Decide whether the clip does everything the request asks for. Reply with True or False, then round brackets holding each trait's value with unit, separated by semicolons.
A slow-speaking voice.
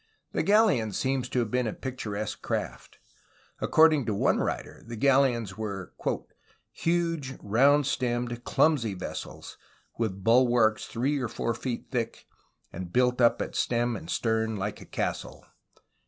False (145 wpm)